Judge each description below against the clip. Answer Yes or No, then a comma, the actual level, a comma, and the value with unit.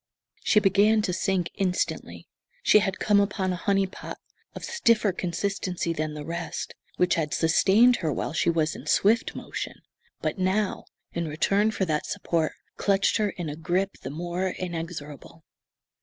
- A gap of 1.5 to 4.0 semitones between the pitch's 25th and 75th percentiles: Yes, average, 3.3 semitones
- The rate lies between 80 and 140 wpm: No, average, 160 wpm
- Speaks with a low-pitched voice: No, medium, 185 Hz